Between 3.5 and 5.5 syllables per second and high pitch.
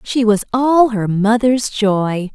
No: 3.2 syllables/s; high, 220 Hz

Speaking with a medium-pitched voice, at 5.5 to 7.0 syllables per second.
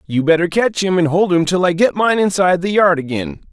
Yes: medium, 175 Hz; 5.7 syllables/s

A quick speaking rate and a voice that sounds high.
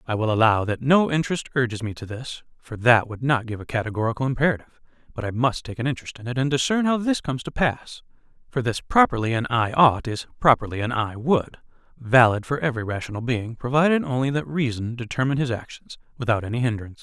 No: fast, 210 wpm; low, 125 Hz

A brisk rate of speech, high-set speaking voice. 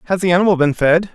No: fast, 260 wpm; medium, 175 Hz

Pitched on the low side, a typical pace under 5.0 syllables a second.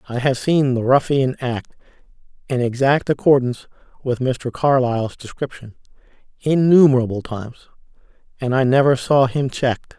No: low, 130 Hz; 5.2 syllables/s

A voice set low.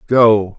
Yes: low, 110 Hz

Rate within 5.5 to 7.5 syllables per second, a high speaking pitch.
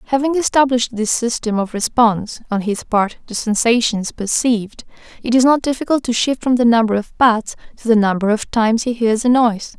Yes: 5.6 syllables/s; high, 230 Hz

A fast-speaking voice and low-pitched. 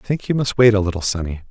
Yes: fast, 320 wpm; low, 105 Hz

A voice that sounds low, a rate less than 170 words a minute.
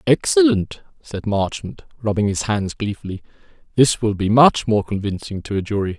Yes: low, 115 Hz; average, 160 wpm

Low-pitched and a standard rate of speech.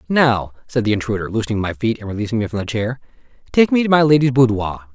No: low, 115 Hz; fast, 230 wpm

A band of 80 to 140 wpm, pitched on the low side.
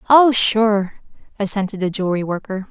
No: slow, 135 wpm; high, 205 Hz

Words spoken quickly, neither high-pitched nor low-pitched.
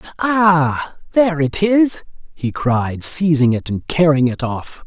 No: average, 150 wpm; medium, 155 Hz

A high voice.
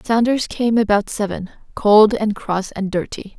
Yes: high, 210 Hz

